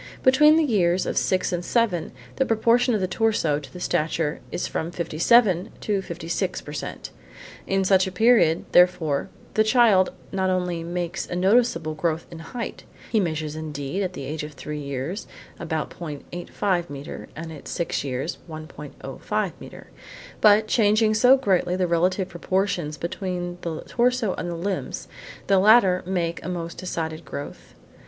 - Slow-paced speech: No, average, 160 wpm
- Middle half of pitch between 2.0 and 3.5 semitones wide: No, average, 4.0 semitones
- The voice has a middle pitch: Yes, medium, 180 Hz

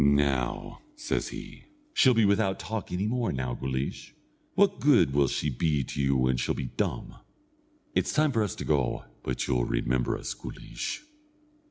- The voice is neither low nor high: No, very low, 70 Hz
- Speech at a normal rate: Yes, average, 170 wpm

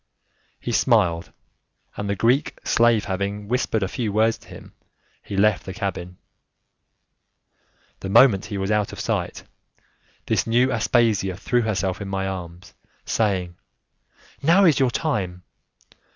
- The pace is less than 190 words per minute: Yes, slow, 135 wpm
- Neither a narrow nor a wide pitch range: Yes, average, 3.4 semitones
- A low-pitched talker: Yes, low, 105 Hz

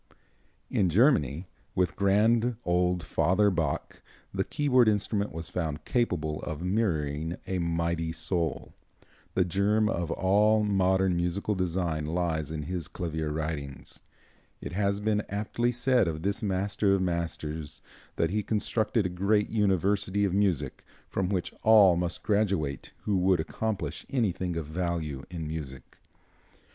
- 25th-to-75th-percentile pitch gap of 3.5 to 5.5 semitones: Yes, average, 3.9 semitones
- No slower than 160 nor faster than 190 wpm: No, slow, 135 wpm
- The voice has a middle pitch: No, very low, 90 Hz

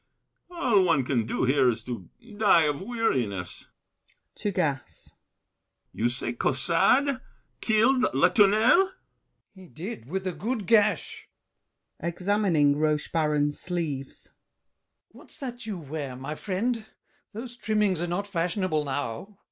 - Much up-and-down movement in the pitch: Yes, wide, 7.0 semitones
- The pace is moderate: No, slow, 125 wpm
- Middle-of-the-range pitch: Yes, medium, 175 Hz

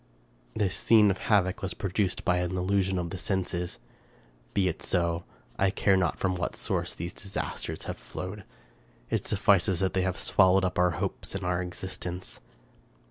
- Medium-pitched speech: No, very low, 95 Hz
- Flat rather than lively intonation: Yes, narrow, 1.5 semitones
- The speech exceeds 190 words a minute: No, average, 170 wpm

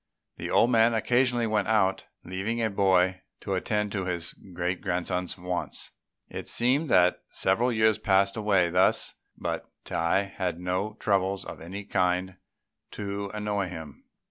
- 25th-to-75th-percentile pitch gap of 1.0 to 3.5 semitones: Yes, average, 2.7 semitones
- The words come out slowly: No, average, 145 wpm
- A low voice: Yes, very low, 95 Hz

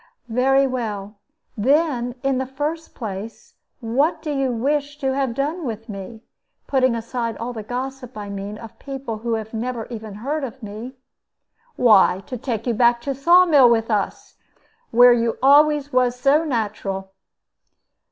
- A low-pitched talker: No, high, 245 Hz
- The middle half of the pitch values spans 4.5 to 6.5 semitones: No, average, 3.5 semitones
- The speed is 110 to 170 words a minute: Yes, average, 160 wpm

